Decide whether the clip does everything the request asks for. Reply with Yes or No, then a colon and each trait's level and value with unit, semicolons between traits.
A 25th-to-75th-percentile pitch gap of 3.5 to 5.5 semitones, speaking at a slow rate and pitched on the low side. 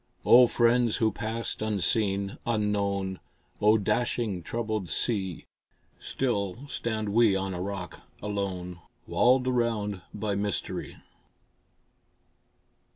No: average, 3.0 semitones; slow, 95 wpm; low, 105 Hz